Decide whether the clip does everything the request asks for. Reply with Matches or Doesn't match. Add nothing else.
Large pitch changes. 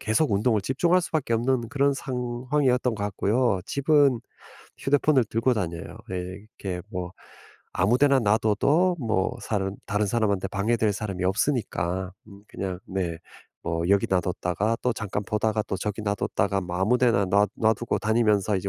Doesn't match